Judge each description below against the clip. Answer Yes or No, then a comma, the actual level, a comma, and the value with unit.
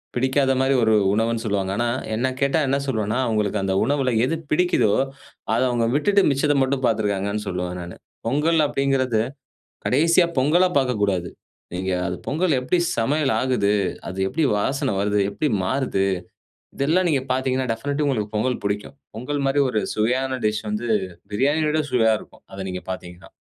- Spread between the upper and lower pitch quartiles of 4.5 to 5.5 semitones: Yes, average, 4.9 semitones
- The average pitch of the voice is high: No, low, 125 Hz